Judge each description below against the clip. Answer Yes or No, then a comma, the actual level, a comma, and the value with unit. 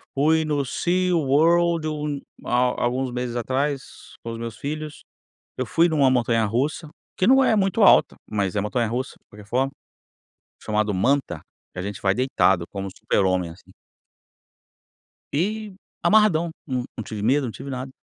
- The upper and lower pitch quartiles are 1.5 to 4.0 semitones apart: No, wide, 5.6 semitones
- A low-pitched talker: Yes, low, 130 Hz